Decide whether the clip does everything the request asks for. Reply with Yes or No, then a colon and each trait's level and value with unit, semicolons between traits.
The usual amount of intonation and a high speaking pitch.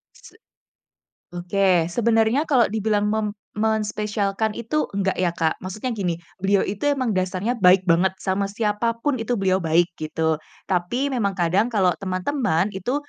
Yes: average, 3.5 semitones; high, 200 Hz